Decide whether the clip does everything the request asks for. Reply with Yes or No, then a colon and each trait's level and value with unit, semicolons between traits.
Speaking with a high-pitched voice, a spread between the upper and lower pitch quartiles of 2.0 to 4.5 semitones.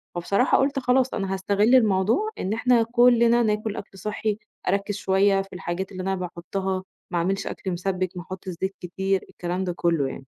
Yes: high, 195 Hz; average, 2.9 semitones